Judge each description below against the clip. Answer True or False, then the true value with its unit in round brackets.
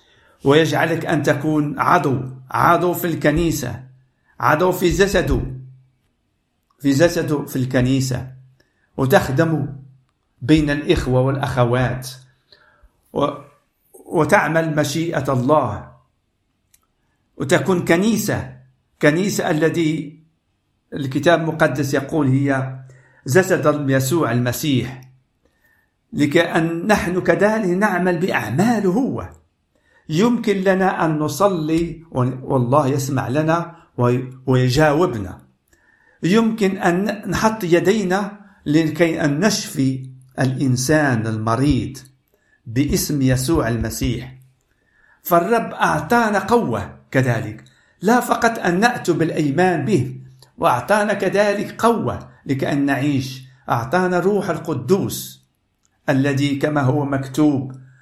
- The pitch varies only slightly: False (5.3 semitones)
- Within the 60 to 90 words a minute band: True (85 wpm)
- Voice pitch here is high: False (150 Hz)